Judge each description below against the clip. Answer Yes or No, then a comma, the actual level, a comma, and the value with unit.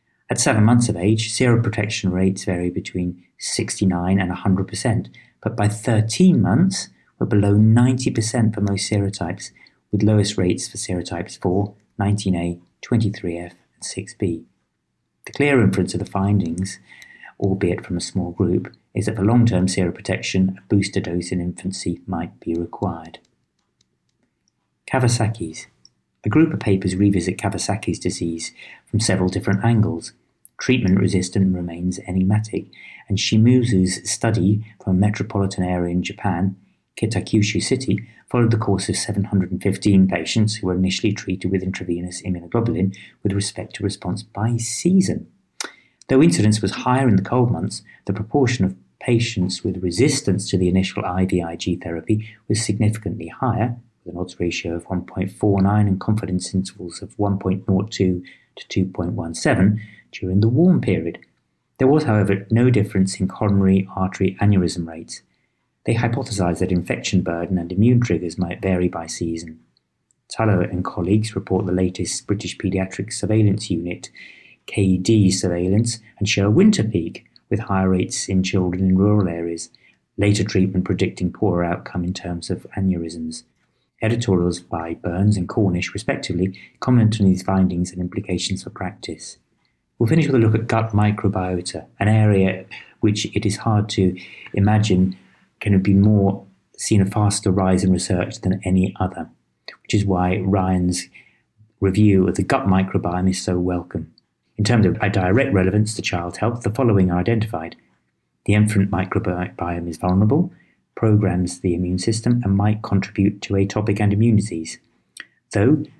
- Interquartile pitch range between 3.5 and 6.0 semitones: No, average, 2.9 semitones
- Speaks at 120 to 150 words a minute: Yes, average, 145 wpm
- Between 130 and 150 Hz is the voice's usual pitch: No, very low, 95 Hz